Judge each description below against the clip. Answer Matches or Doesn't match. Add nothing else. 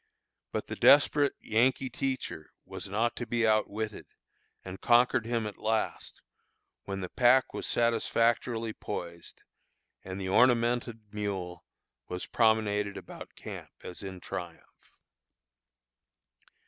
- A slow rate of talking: Matches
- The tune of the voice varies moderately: Matches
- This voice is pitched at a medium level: Doesn't match